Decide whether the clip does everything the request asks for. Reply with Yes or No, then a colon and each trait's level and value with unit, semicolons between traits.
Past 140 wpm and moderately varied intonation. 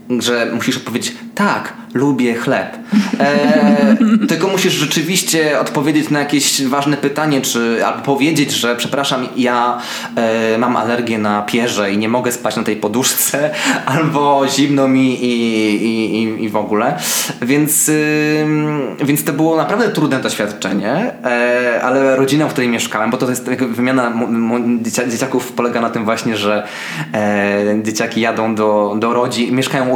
Yes: average, 150 wpm; average, 4.1 semitones